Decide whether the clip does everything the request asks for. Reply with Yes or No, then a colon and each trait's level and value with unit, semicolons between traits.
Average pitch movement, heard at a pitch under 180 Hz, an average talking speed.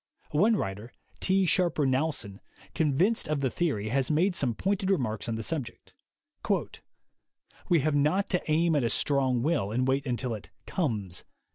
No: wide, 6.2 semitones; medium, 140 Hz; average, 160 wpm